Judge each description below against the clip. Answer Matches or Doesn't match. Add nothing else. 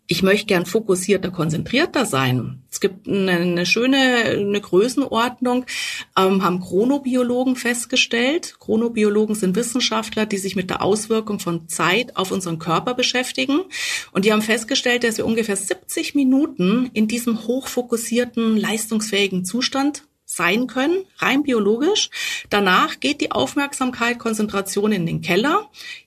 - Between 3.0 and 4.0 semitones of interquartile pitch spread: Doesn't match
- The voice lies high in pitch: Matches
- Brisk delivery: Doesn't match